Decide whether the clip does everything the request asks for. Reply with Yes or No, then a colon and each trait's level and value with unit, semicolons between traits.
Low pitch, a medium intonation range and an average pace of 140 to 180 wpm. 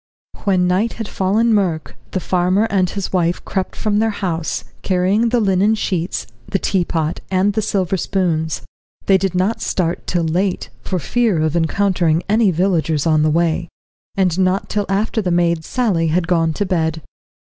No: medium, 185 Hz; average, 3.0 semitones; average, 170 wpm